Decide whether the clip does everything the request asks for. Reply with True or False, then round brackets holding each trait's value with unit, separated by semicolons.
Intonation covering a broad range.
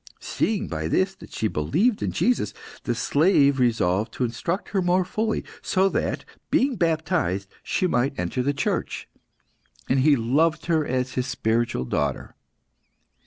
True (7.6 semitones)